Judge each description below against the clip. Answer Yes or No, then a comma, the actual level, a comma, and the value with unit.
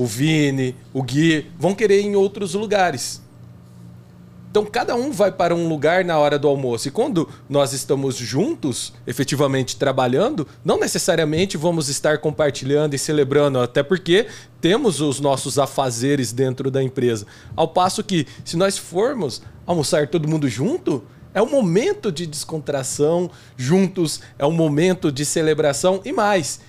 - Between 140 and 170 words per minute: Yes, average, 150 wpm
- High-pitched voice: No, medium, 150 Hz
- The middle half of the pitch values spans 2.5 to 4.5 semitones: No, average, 5.0 semitones